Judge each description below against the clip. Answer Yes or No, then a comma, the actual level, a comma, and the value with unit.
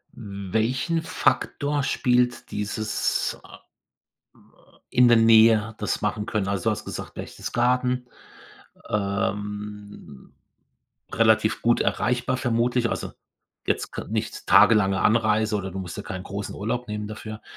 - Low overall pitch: Yes, low, 110 Hz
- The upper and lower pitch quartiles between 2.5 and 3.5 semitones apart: Yes, average, 2.9 semitones